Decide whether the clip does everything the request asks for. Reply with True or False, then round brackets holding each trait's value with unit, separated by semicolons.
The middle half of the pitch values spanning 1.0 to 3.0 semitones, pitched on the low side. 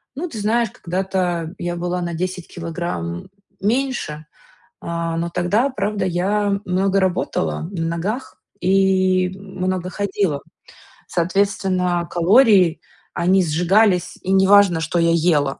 False (2.6 semitones; 185 Hz)